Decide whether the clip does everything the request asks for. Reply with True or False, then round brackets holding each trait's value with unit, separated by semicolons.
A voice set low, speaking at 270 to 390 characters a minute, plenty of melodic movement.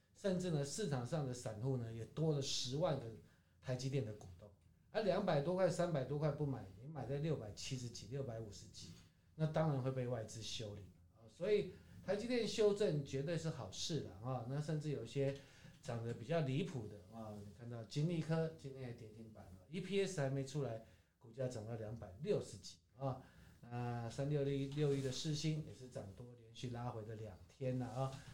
False (130 Hz; 295 characters per minute; 5.0 semitones)